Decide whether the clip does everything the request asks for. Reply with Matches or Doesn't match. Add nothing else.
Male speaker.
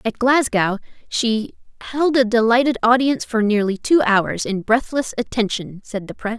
Doesn't match